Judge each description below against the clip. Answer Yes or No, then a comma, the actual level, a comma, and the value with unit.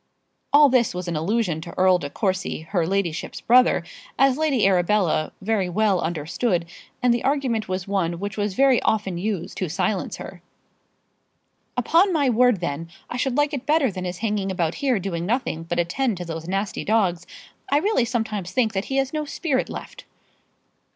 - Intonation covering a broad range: Yes, wide, 6.1 semitones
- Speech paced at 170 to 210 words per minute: Yes, average, 180 wpm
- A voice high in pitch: Yes, high, 205 Hz